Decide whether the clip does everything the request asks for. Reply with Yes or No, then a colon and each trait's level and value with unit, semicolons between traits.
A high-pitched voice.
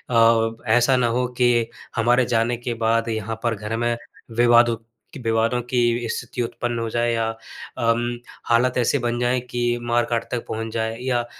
No: low, 120 Hz